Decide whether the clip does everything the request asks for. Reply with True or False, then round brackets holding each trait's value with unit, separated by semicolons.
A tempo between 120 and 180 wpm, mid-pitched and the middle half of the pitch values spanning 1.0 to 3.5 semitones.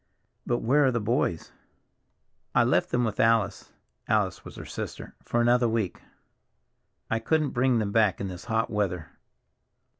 False (145 wpm; 115 Hz; 2.8 semitones)